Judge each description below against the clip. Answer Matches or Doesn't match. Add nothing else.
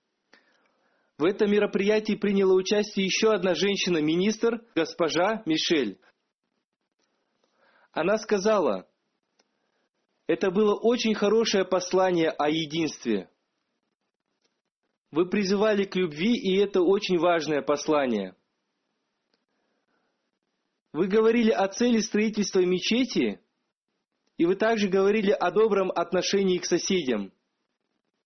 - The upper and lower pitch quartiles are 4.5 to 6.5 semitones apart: Doesn't match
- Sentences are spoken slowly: Matches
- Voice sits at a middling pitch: Doesn't match